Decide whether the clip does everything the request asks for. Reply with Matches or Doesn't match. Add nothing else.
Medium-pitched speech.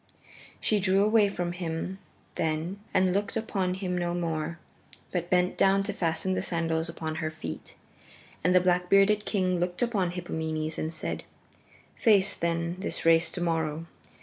Matches